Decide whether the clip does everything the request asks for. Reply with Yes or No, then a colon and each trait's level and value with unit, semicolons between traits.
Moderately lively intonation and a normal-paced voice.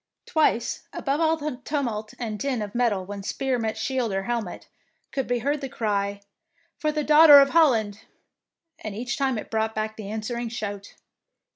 Yes: average, 4.5 semitones; average, 180 wpm